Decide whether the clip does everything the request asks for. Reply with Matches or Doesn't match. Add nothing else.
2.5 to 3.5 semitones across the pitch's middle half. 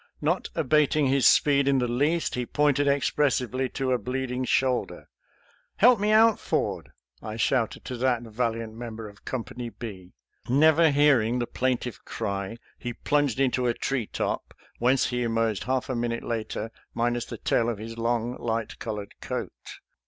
Matches